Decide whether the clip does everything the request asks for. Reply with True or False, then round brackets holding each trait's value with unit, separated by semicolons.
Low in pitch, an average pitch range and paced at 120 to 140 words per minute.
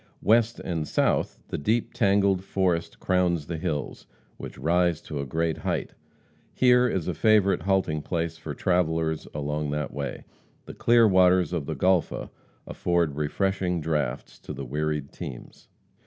False (85 Hz; 3.8 semitones; 150 wpm)